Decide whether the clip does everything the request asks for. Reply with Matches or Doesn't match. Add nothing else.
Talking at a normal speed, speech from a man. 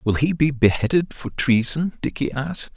Matches